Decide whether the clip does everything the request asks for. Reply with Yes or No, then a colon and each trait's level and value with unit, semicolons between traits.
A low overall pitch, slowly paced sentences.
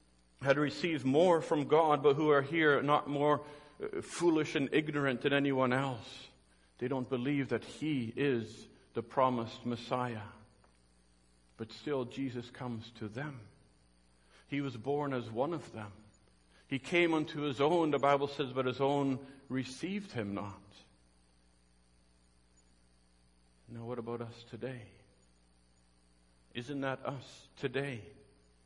Yes: low, 120 Hz; slow, 130 wpm